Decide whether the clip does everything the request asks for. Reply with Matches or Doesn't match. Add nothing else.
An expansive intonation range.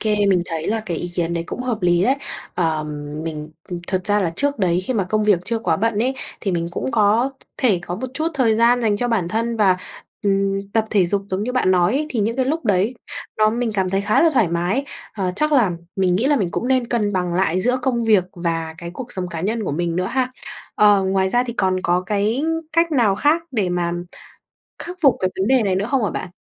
Doesn't match